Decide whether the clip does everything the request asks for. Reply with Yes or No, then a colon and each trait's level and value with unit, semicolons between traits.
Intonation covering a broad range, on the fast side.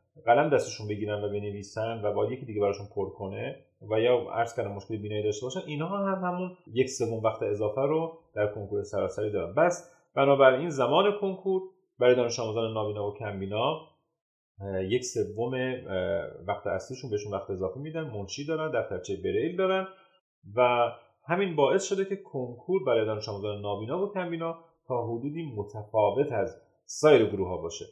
Yes: wide, 8.0 semitones; fast, 170 wpm